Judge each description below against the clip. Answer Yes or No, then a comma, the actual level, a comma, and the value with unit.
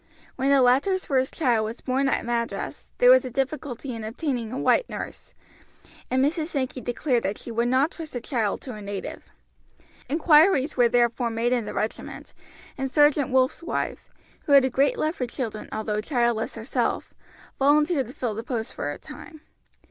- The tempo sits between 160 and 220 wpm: Yes, average, 185 wpm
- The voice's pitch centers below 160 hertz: No, very high, 255 Hz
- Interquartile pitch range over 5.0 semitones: No, average, 3.6 semitones